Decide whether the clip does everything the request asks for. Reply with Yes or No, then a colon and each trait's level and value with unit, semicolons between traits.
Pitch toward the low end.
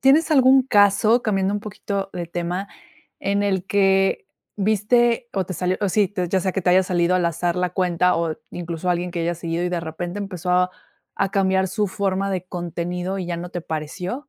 No: medium, 185 Hz